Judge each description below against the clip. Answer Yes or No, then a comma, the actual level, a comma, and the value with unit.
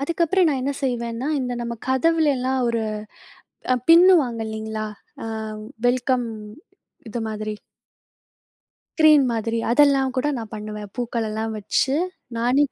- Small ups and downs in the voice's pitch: No, average, 4.0 semitones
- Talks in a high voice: Yes, high, 245 Hz